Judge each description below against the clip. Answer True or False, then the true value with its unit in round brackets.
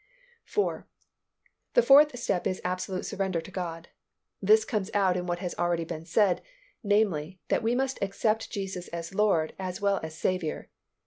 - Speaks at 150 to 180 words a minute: True (165 wpm)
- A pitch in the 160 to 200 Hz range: True (190 Hz)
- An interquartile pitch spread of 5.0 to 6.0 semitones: False (3.3 semitones)